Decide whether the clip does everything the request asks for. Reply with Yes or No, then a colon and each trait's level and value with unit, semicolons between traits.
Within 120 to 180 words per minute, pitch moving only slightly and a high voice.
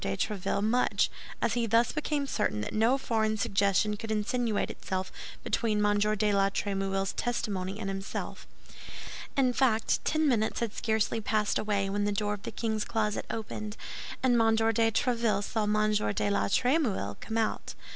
Yes: average, 165 wpm; narrow, 2.1 semitones; high, 215 Hz